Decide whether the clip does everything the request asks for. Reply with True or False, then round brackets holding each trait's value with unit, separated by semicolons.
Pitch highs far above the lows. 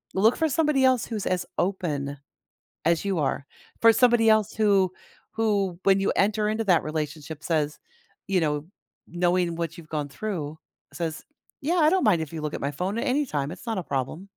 True (5.8 semitones)